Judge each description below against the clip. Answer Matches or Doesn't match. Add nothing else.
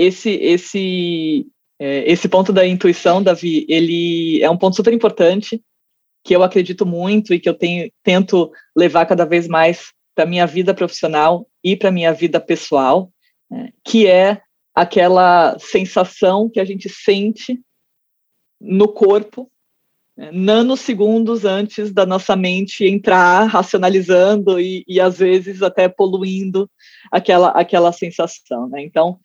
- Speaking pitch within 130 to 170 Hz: Doesn't match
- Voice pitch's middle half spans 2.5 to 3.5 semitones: Matches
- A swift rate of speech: Doesn't match